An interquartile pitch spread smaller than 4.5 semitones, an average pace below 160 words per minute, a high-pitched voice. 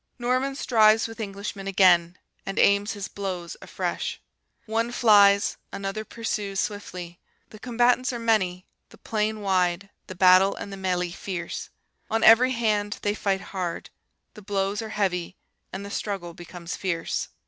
Yes: average, 2.8 semitones; average, 150 wpm; high, 200 Hz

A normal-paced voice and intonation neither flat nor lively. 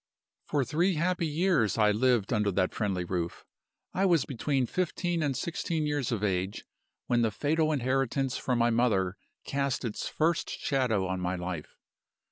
No: average, 160 wpm; wide, 6.6 semitones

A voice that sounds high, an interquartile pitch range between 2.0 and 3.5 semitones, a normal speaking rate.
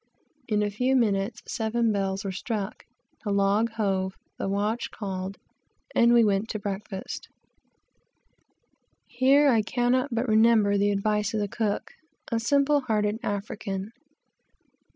No: high, 210 Hz; average, 2.7 semitones; slow, 130 wpm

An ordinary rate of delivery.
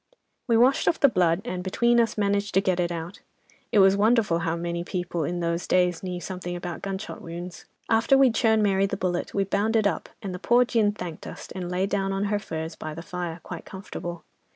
No: fast, 225 wpm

